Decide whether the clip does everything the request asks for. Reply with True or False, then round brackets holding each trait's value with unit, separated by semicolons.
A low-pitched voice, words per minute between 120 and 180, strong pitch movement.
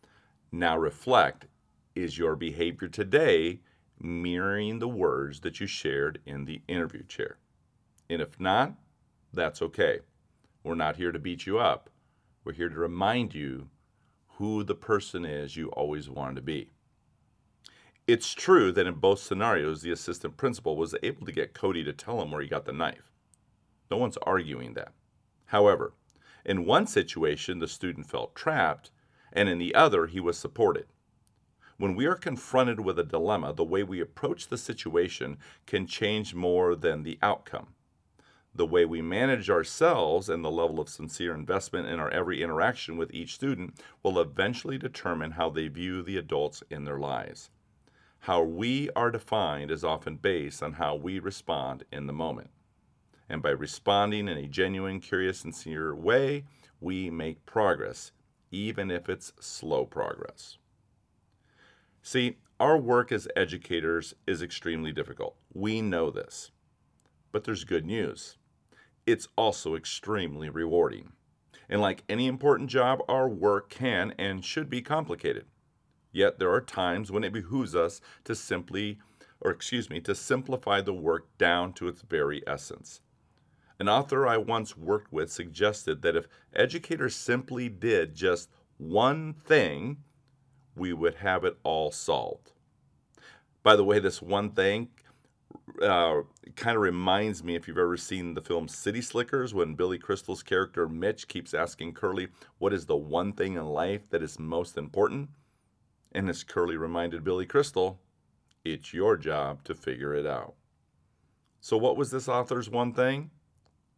True (95 Hz; 155 wpm; 6.4 semitones)